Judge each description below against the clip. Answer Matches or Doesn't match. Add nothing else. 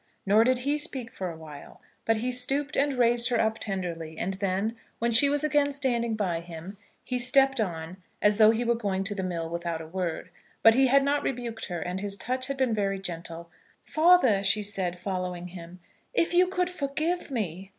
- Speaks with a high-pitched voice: Matches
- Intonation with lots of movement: Matches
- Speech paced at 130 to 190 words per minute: Doesn't match